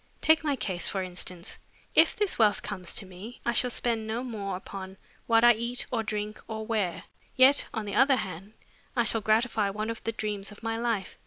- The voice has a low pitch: No, high, 220 Hz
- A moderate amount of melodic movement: Yes, average, 3.0 semitones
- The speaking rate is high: Yes, fast, 210 wpm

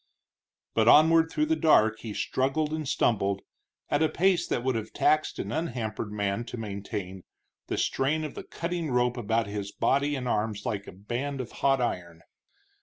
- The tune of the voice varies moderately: No, wide, 6.2 semitones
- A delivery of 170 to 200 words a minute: Yes, average, 180 wpm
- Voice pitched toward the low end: Yes, low, 120 Hz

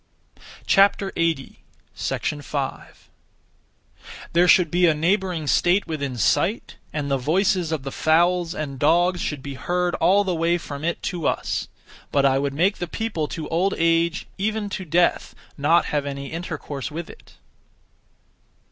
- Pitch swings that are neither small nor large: Yes, average, 3.5 semitones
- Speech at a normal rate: Yes, average, 145 wpm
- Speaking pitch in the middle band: Yes, medium, 165 Hz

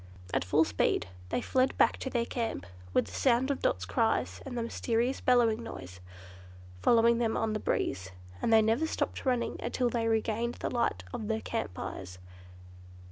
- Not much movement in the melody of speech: Yes, narrow, 2.1 semitones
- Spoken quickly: No, average, 180 wpm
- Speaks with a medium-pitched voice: No, high, 230 Hz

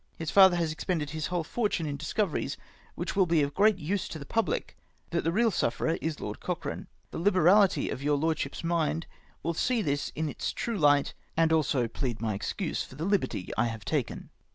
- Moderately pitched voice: Yes, medium, 160 Hz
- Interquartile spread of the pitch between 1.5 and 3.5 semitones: No, average, 4.2 semitones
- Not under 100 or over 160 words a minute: No, fast, 205 wpm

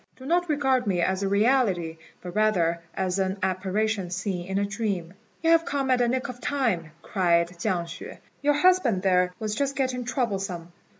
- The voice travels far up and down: Yes, wide, 6.0 semitones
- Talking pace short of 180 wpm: No, average, 185 wpm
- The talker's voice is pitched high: Yes, high, 200 Hz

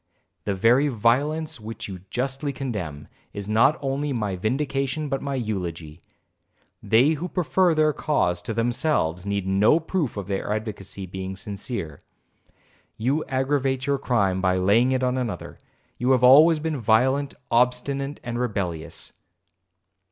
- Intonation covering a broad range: Yes, wide, 5.7 semitones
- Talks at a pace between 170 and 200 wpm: No, average, 140 wpm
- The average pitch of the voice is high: No, low, 125 Hz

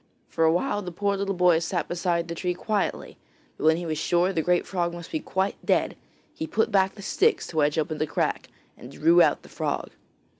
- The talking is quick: Yes, fast, 220 wpm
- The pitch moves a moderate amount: Yes, average, 3.1 semitones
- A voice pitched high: No, medium, 175 Hz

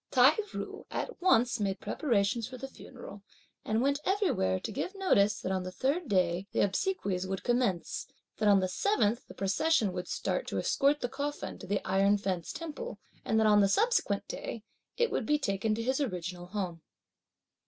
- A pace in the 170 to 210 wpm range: Yes, average, 185 wpm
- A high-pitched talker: Yes, high, 220 Hz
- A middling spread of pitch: No, wide, 6.7 semitones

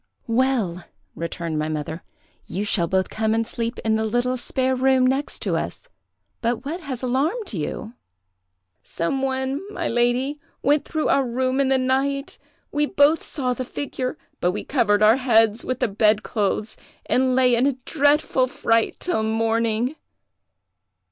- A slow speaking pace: No, average, 155 wpm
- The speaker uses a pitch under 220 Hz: No, very high, 250 Hz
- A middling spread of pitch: Yes, average, 3.5 semitones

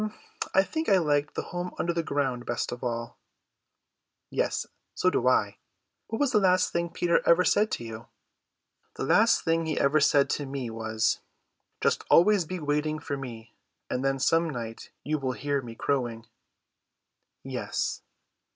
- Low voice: No, medium, 145 Hz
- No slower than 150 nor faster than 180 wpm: Yes, average, 165 wpm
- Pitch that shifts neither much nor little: No, wide, 5.8 semitones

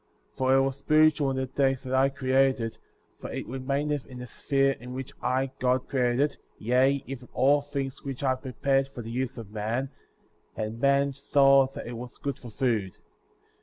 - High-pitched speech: No, low, 130 Hz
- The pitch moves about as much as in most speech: No, narrow, 1.7 semitones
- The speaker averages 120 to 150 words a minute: No, average, 200 wpm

